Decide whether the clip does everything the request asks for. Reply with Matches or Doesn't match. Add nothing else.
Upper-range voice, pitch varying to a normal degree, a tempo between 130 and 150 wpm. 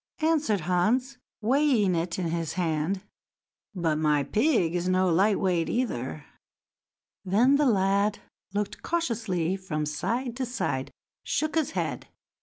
Doesn't match